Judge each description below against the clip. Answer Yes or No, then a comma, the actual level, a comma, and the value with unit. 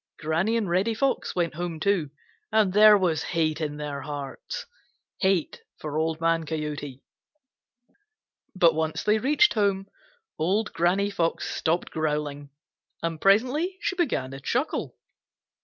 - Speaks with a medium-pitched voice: Yes, medium, 170 Hz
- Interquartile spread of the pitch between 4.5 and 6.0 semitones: Yes, average, 5.2 semitones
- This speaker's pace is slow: Yes, slow, 130 wpm